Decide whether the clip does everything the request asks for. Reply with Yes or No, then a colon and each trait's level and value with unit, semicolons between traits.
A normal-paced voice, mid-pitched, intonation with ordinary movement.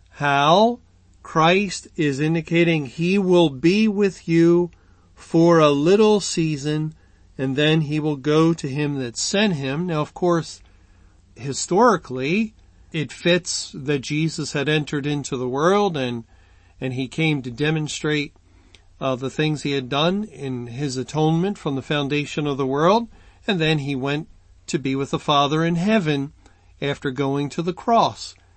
Yes: average, 155 wpm; medium, 150 Hz; average, 4.1 semitones